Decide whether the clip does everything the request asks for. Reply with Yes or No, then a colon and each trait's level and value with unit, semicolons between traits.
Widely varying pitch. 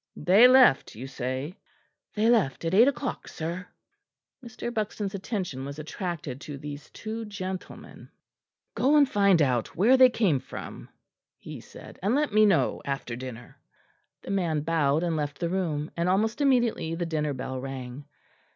Yes: wide, 6.9 semitones